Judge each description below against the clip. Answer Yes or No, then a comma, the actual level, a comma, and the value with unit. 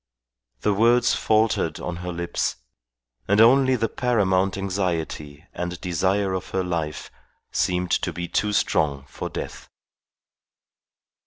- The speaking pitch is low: Yes, very low, 95 Hz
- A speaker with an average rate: No, slow, 120 wpm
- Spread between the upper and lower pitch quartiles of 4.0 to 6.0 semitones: No, average, 3.3 semitones